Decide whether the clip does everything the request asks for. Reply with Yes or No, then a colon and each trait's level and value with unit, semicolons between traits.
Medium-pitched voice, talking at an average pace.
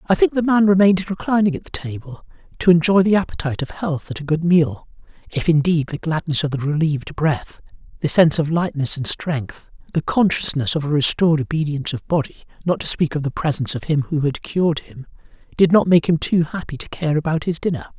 No: medium, 160 Hz; fast, 215 wpm